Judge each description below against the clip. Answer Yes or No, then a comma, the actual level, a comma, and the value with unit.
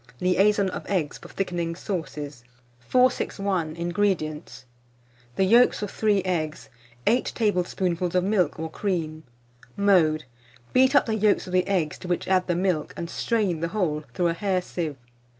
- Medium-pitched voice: Yes, medium, 180 Hz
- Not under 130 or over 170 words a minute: Yes, average, 155 wpm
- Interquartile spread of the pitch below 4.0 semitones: Yes, average, 3.4 semitones